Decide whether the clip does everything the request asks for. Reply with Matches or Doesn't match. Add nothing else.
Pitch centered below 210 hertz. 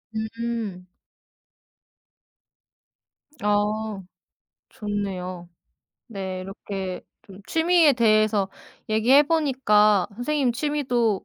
Doesn't match